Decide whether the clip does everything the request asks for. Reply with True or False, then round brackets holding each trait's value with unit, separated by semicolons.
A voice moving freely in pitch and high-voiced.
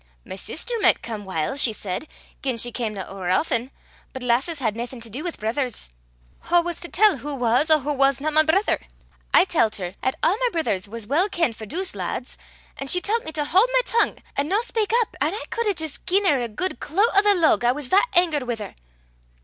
True (7.4 semitones; 285 Hz)